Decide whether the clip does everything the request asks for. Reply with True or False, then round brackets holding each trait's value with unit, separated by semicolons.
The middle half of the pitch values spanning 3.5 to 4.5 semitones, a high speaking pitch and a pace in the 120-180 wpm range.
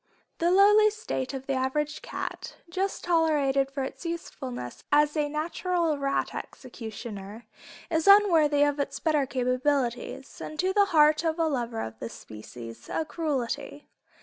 True (4.2 semitones; 290 Hz; 150 wpm)